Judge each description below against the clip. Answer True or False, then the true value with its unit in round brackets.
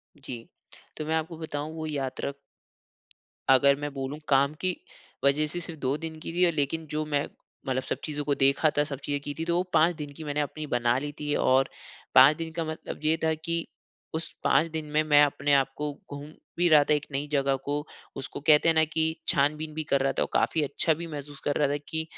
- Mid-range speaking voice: True (150 Hz)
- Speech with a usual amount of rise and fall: False (2.1 semitones)